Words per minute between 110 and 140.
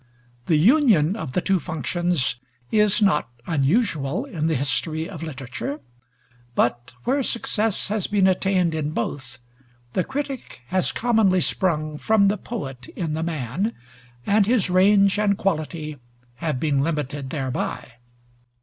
Yes: slow, 135 wpm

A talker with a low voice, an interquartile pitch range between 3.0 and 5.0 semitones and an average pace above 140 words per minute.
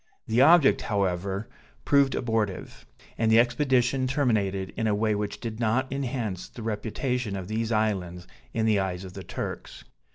Yes: low, 110 Hz; average, 3.9 semitones; average, 160 wpm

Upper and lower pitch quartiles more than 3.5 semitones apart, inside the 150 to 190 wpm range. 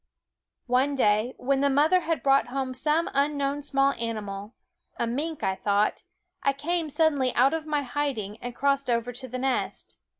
No: average, 3.2 semitones; average, 170 wpm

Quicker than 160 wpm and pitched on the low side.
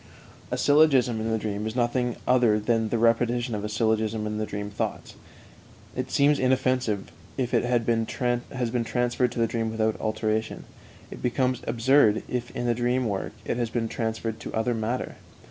Yes: average, 180 wpm; low, 115 Hz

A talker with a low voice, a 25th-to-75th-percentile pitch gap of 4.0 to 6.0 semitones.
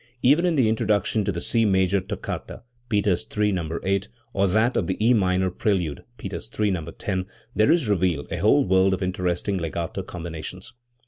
No: very low, 95 Hz; average, 2.8 semitones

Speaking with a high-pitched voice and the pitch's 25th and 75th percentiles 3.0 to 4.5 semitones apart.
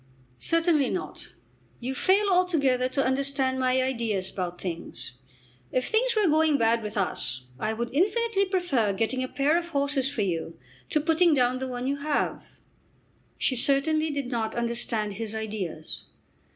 No: very high, 260 Hz; wide, 5.6 semitones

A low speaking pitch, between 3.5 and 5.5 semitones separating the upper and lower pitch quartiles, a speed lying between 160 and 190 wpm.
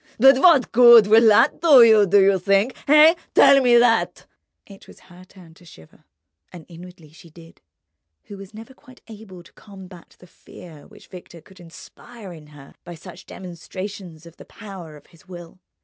No: high, 190 Hz; average, 4.8 semitones; average, 180 wpm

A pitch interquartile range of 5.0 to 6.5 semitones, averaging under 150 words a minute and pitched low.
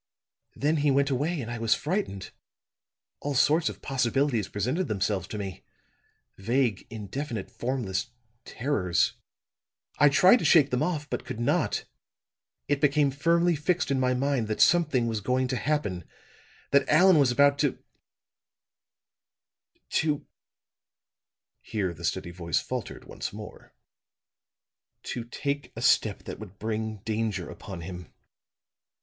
Yes: average, 5.3 semitones; slow, 135 wpm; low, 125 Hz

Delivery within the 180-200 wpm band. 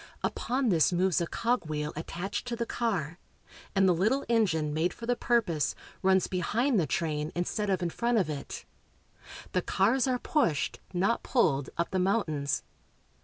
No: average, 165 wpm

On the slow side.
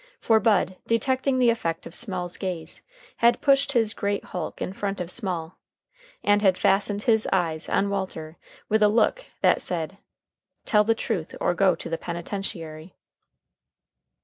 No: average, 150 wpm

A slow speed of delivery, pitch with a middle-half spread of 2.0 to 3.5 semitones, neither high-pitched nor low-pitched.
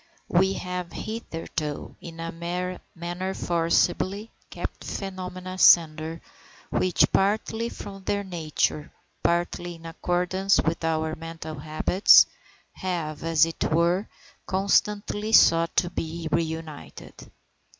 Yes: slow, 105 wpm; narrow, 2.4 semitones; medium, 175 Hz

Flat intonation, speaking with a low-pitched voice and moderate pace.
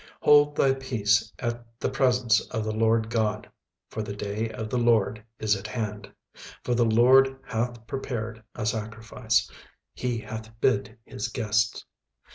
Yes: narrow, 2.2 semitones; low, 115 Hz; average, 155 wpm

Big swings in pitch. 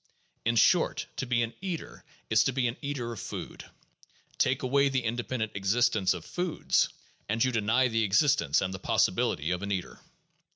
No: average, 4.4 semitones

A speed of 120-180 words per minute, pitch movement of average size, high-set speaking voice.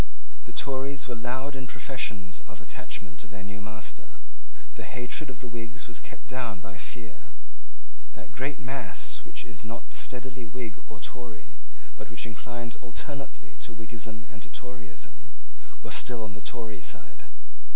No: average, 160 wpm; average, 3.2 semitones; low, 115 Hz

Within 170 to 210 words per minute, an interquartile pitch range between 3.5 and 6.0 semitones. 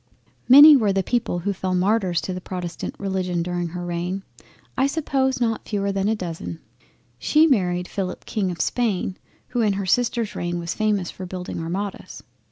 Yes: average, 175 wpm; average, 3.9 semitones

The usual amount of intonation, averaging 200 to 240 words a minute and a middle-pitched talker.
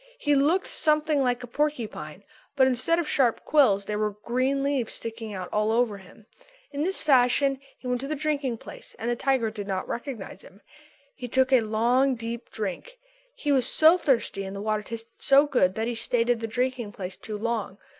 No: average, 4.2 semitones; fast, 205 wpm; high, 245 Hz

